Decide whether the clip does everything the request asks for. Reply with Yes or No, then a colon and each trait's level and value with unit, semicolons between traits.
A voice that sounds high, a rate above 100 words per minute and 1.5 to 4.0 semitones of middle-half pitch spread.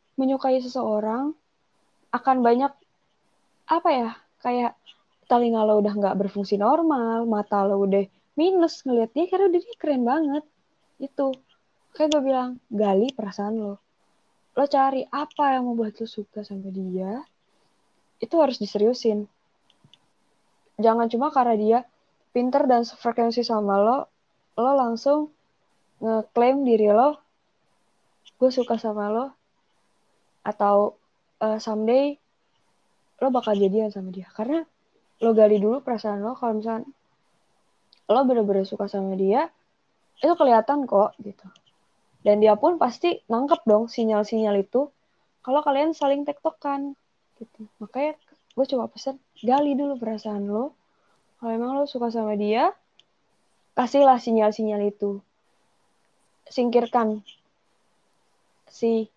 No: high, 235 Hz; average, 120 wpm; average, 4.5 semitones